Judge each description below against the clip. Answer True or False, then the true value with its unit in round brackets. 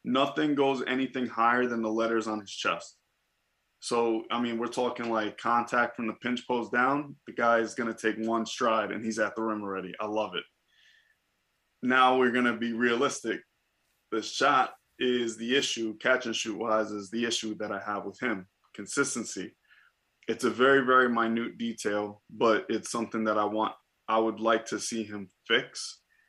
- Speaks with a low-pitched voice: True (115 Hz)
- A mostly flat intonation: True (2.1 semitones)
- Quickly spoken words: False (185 wpm)